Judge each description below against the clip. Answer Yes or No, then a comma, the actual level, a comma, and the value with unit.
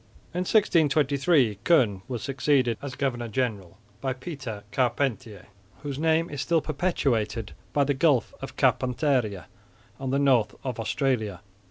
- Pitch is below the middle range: Yes, low, 130 Hz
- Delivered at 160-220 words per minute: No, slow, 135 wpm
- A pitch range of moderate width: Yes, average, 4.0 semitones